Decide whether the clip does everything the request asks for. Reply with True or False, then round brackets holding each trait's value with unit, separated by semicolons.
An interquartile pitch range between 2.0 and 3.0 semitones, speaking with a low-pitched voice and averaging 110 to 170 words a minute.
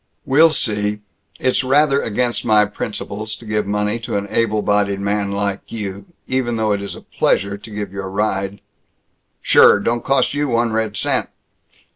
False (2.6 semitones; 105 Hz; 180 wpm)